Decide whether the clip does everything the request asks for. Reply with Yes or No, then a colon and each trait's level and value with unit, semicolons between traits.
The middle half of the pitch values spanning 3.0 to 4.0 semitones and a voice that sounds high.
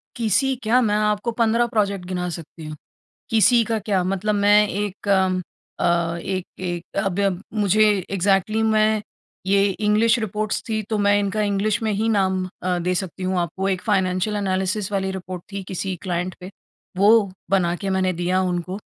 No: narrow, 2.5 semitones; high, 195 Hz